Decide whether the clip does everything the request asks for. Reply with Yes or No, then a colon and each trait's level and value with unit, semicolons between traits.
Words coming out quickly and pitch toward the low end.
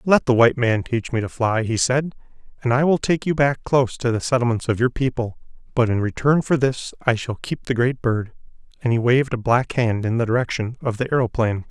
Yes: fast, 235 wpm; low, 125 Hz